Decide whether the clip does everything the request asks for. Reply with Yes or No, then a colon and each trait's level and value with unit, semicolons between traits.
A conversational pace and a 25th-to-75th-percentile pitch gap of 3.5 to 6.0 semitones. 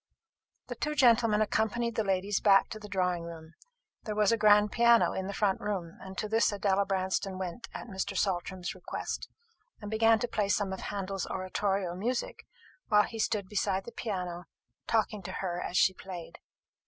No: average, 180 wpm; narrow, 2.5 semitones